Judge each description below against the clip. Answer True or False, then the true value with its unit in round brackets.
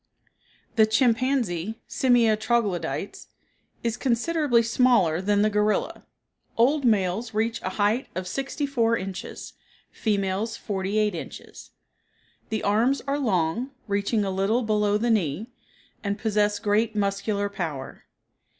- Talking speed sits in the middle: False (125 wpm)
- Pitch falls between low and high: False (215 Hz)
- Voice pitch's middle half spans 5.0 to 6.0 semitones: False (2.9 semitones)